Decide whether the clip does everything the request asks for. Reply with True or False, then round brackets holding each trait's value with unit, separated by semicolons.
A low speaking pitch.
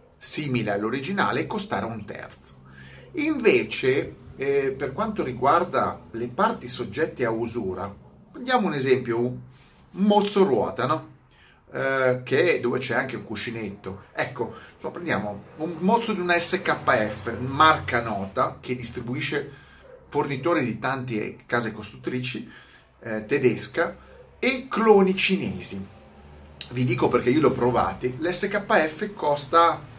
True (130 Hz)